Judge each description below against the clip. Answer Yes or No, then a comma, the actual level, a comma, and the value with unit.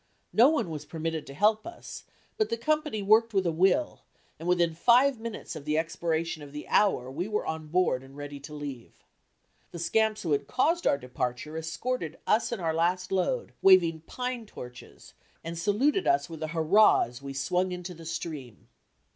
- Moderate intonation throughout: No, wide, 6.1 semitones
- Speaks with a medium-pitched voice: Yes, medium, 170 Hz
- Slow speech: No, average, 190 wpm